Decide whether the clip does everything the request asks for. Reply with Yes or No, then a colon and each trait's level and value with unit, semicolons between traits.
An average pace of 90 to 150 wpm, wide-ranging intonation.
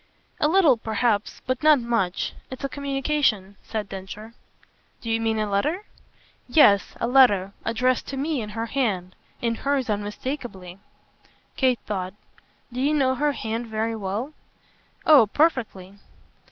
No: average, 140 wpm; average, 4.7 semitones